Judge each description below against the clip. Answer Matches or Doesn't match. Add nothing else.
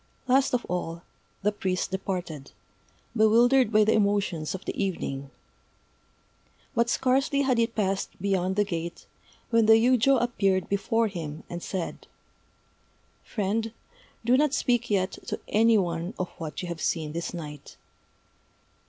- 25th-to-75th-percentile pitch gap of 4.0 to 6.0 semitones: Matches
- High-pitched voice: Matches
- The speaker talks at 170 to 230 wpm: Doesn't match